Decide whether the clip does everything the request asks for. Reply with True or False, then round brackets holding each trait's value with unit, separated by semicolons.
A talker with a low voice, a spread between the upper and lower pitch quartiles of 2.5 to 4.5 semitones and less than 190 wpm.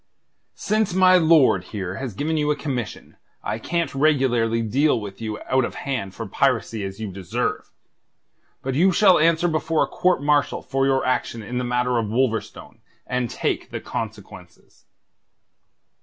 False (130 Hz; 5.6 semitones; 160 wpm)